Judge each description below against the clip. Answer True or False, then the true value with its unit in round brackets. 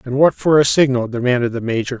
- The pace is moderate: False (240 wpm)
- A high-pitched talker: False (130 Hz)